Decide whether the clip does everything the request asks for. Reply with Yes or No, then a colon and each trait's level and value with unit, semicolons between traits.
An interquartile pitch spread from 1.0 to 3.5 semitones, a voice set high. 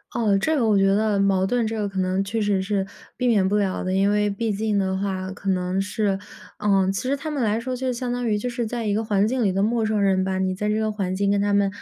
Yes: narrow, 2.4 semitones; high, 205 Hz